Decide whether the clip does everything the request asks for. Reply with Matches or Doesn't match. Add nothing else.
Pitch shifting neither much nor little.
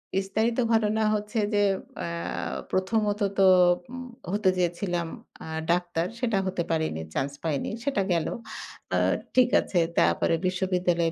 Matches